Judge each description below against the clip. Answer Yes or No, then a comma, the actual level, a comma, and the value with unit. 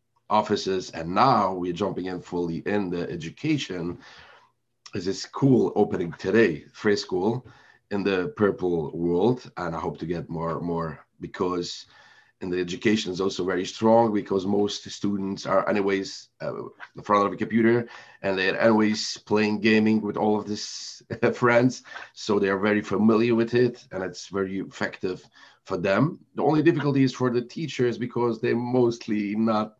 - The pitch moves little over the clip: No, average, 3.5 semitones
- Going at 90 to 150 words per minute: No, average, 165 wpm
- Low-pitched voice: Yes, low, 105 Hz